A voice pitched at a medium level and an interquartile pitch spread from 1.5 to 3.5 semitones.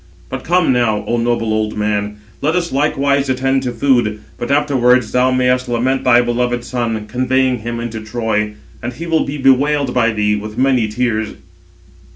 No: low, 125 Hz; average, 3.2 semitones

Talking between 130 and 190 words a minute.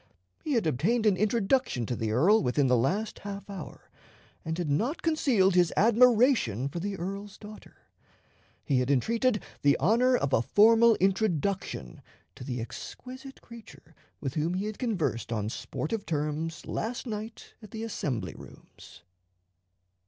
Yes: average, 150 wpm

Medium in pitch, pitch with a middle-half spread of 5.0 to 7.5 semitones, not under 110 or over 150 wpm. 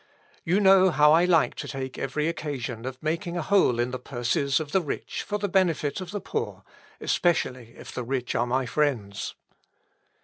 No: medium, 150 Hz; wide, 5.5 semitones; average, 190 wpm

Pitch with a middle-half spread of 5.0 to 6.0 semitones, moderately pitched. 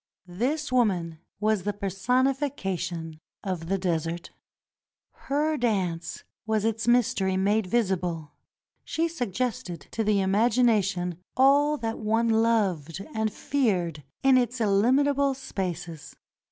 No: wide, 5.5 semitones; high, 210 Hz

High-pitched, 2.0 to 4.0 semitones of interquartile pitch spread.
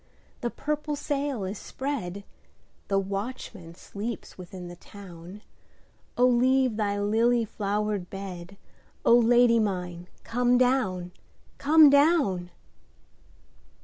No: high, 210 Hz; average, 4.7 semitones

